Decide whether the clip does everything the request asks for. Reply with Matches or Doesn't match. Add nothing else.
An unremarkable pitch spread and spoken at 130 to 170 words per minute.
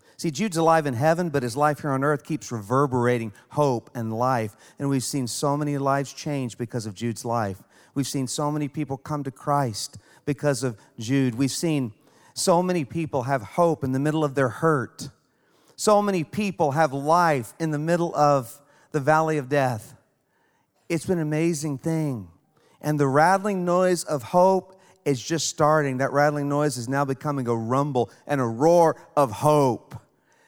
Doesn't match